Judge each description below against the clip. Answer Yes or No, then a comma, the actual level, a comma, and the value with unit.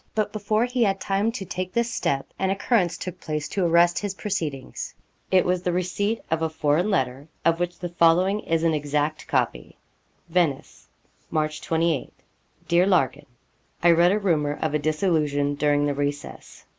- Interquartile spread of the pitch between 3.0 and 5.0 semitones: Yes, average, 4.2 semitones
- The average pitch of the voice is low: No, medium, 170 Hz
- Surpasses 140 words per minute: Yes, average, 170 wpm